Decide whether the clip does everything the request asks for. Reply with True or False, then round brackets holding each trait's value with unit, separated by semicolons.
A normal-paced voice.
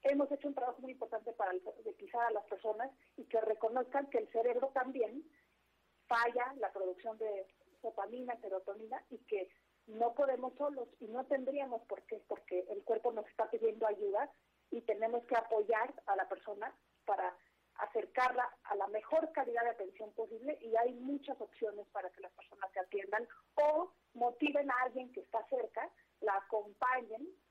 True (165 wpm)